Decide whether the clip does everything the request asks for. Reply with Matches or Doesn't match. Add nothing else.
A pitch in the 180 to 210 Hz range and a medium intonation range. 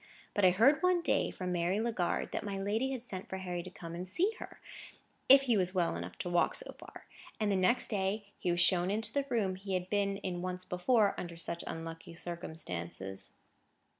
Matches